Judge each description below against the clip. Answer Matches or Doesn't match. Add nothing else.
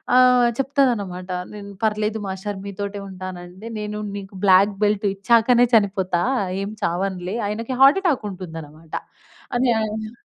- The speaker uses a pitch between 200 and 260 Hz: Matches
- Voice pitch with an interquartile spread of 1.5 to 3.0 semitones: Doesn't match